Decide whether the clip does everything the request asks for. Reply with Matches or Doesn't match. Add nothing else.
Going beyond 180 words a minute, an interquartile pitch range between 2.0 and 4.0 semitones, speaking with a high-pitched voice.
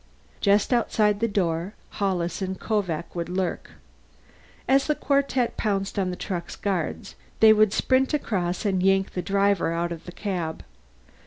Doesn't match